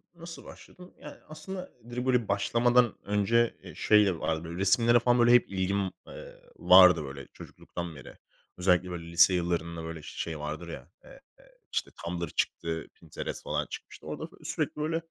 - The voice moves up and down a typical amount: No, wide, 6.0 semitones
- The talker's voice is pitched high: No, very low, 95 Hz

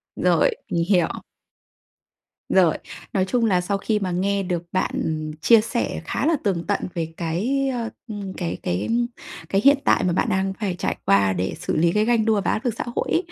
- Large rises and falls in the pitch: No, average, 4.4 semitones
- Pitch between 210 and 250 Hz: No, high, 195 Hz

